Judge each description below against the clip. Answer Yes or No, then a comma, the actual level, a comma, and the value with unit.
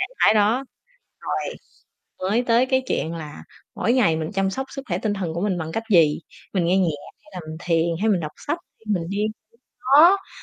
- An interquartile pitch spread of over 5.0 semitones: Yes, wide, 5.5 semitones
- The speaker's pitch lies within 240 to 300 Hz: No, high, 195 Hz